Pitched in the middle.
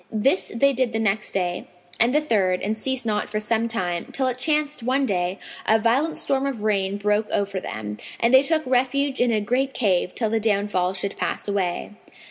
No: high, 220 Hz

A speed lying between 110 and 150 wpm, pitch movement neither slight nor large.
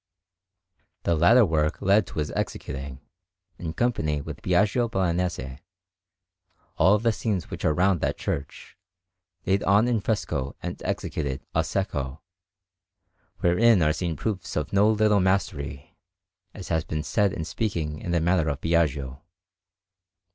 Yes: average, 140 wpm; average, 4.9 semitones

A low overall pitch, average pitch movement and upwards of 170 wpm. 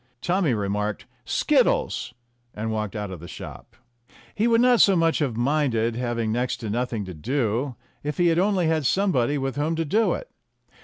No: low, 130 Hz; wide, 6.8 semitones; average, 185 wpm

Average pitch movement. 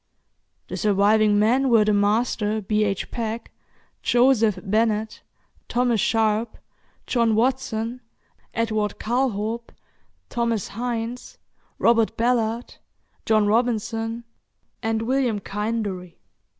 No: narrow, 1.9 semitones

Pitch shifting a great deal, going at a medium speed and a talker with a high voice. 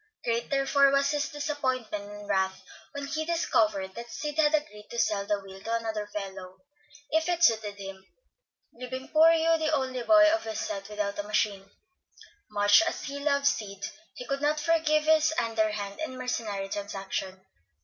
Yes: wide, 6.4 semitones; average, 170 wpm; high, 235 Hz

